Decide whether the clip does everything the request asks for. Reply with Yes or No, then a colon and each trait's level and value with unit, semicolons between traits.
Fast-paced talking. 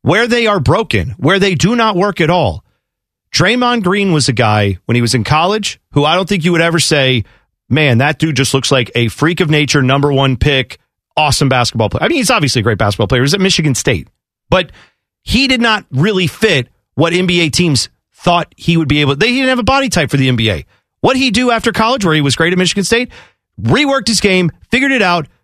Yes: fast, 235 wpm